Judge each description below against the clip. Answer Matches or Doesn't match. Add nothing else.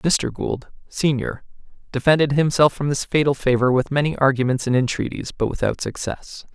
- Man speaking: Matches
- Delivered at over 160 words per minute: Doesn't match